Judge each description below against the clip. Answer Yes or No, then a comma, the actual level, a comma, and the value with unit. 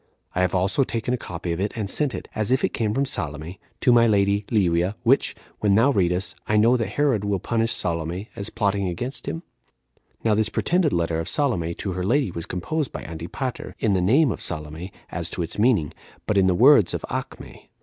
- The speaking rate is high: Yes, fast, 210 wpm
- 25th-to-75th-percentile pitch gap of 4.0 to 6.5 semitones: Yes, average, 5.1 semitones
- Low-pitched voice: Yes, low, 100 Hz